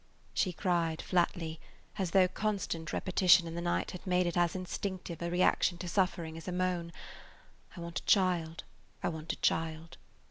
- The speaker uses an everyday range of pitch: No, narrow, 1.7 semitones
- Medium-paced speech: Yes, average, 175 wpm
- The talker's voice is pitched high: No, medium, 175 Hz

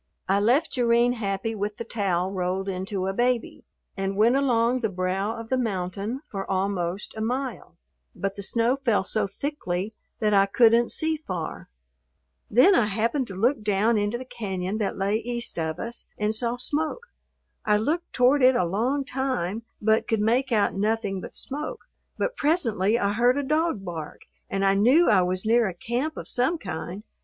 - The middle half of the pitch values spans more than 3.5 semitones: Yes, average, 4.3 semitones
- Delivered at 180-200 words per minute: Yes, average, 185 wpm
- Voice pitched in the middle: No, high, 220 Hz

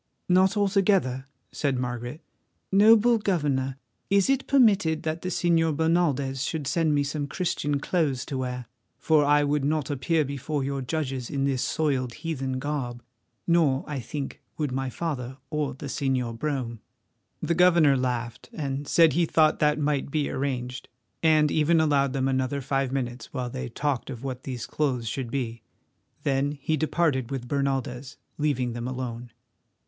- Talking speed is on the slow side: No, average, 160 wpm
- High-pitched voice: No, medium, 140 Hz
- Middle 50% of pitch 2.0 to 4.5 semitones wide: Yes, average, 3.4 semitones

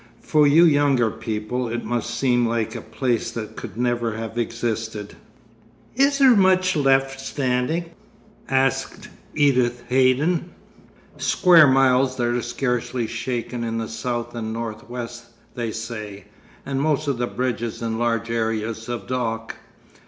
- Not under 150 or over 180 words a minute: No, average, 140 wpm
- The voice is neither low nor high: No, low, 120 Hz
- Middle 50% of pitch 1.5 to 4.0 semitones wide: Yes, average, 2.8 semitones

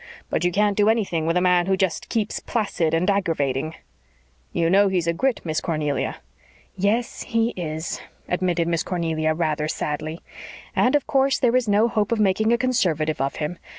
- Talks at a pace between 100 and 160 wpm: No, average, 185 wpm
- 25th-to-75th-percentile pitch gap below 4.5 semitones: No, average, 4.9 semitones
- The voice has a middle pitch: Yes, medium, 180 Hz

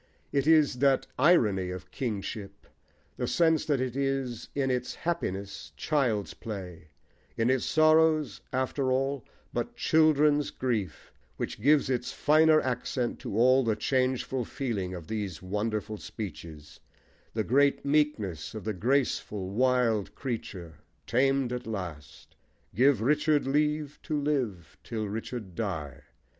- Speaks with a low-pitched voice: Yes, low, 125 Hz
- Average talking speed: No, slow, 130 wpm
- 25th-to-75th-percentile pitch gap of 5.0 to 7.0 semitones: Yes, wide, 5.6 semitones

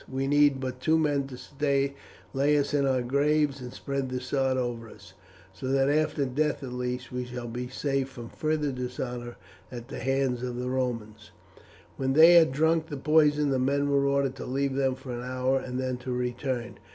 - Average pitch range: No, narrow, 2.1 semitones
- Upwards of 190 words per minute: Yes, average, 200 wpm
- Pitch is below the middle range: Yes, low, 130 Hz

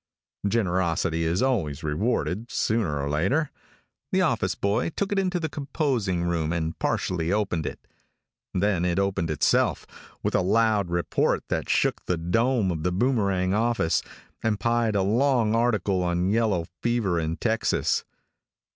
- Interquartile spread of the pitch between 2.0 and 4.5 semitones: No, average, 5.2 semitones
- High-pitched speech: No, low, 100 Hz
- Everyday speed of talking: Yes, average, 145 wpm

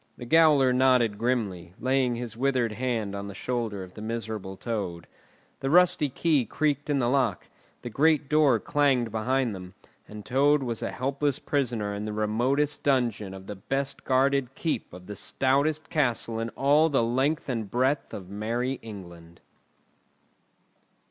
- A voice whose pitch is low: Yes, low, 125 Hz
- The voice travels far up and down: No, average, 4.5 semitones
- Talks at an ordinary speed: Yes, average, 160 wpm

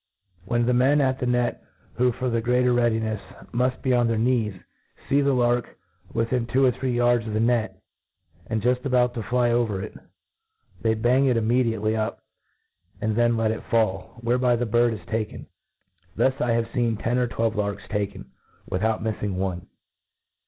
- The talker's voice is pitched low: Yes, low, 120 Hz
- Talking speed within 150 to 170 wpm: No, average, 180 wpm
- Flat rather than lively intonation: Yes, narrow, 2.1 semitones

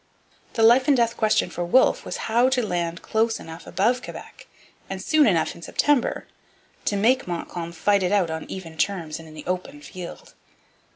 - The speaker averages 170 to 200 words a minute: Yes, average, 185 wpm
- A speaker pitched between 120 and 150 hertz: No, high, 195 Hz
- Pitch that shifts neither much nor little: No, wide, 5.7 semitones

